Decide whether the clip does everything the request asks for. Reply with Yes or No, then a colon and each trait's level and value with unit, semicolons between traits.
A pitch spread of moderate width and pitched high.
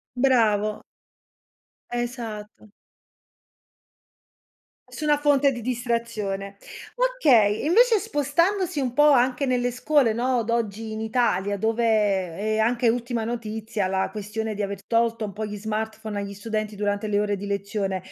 Yes: average, 3.1 semitones; high, 225 Hz